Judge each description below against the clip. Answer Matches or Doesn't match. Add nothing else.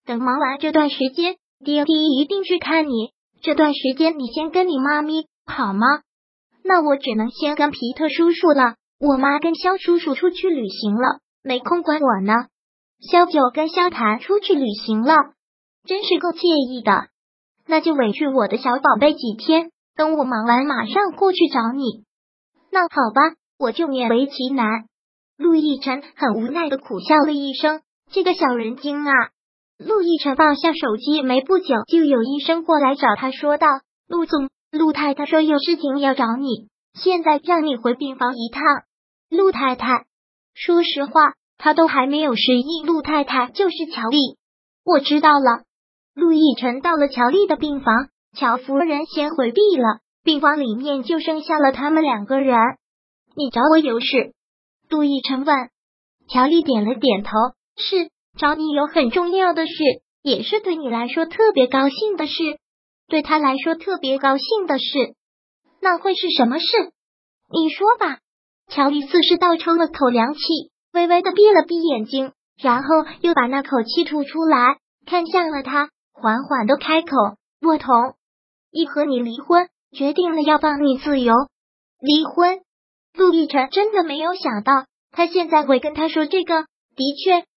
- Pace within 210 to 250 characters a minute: Matches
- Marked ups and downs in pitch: Doesn't match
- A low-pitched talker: Doesn't match